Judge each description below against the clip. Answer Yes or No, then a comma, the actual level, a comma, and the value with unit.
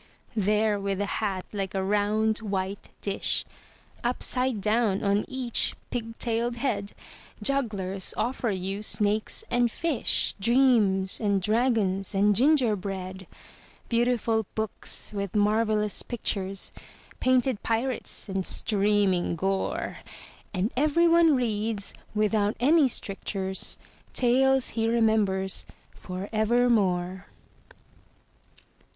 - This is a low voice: No, high, 215 Hz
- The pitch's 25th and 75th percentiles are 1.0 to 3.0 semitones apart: No, average, 3.4 semitones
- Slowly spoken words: Yes, slow, 100 wpm